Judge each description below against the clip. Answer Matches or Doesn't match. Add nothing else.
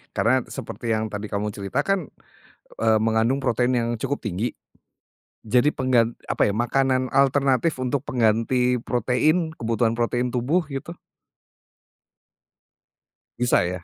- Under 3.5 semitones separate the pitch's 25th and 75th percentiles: Matches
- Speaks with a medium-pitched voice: Doesn't match